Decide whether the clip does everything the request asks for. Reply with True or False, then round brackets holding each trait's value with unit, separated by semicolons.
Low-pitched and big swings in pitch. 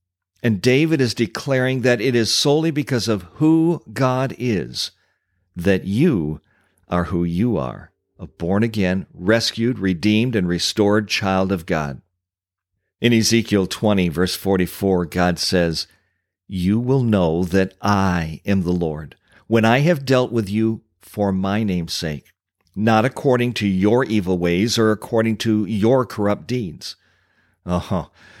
False (100 Hz; 4.0 semitones)